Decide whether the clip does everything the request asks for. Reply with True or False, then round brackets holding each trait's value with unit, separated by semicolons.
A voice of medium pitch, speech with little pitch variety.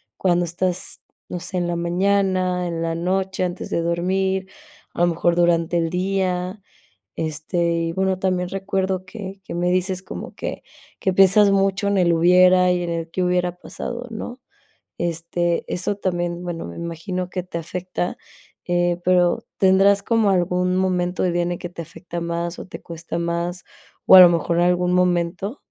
True (180 Hz; 1.6 semitones)